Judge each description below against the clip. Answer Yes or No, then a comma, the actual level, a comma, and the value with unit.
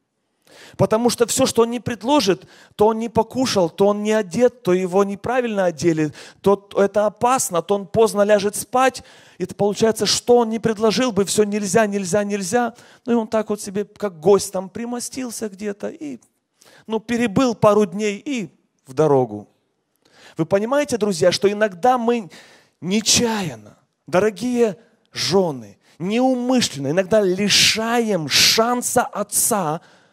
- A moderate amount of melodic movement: Yes, average, 3.3 semitones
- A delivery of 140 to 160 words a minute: Yes, average, 145 wpm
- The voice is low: No, high, 210 Hz